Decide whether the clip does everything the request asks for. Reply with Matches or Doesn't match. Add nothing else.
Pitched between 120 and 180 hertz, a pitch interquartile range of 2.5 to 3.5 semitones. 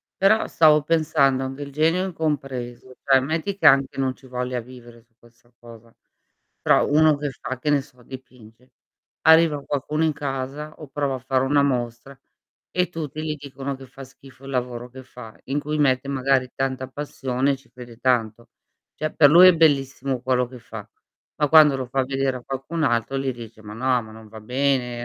Matches